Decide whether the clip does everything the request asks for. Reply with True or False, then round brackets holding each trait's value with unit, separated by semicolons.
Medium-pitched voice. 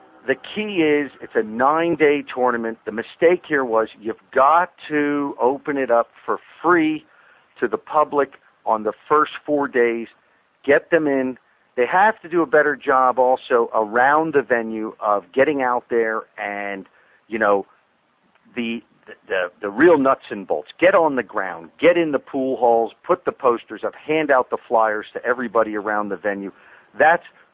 False (125 Hz)